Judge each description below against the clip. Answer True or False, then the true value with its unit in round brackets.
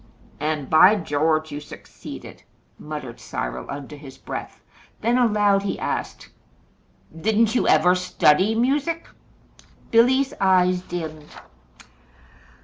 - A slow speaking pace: True (105 wpm)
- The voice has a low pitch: False (180 Hz)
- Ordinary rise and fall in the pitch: False (6.6 semitones)